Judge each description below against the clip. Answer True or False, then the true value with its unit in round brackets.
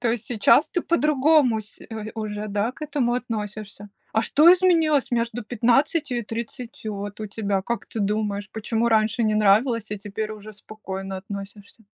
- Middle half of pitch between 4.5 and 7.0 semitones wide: False (2.9 semitones)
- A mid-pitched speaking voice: False (220 Hz)